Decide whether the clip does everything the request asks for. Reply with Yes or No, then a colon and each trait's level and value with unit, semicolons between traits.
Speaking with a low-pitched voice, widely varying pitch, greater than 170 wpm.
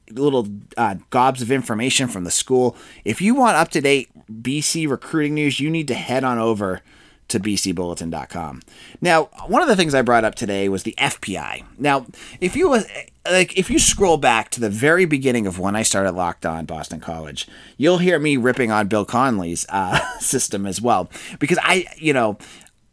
Yes: low, 120 Hz; wide, 6.8 semitones; average, 190 wpm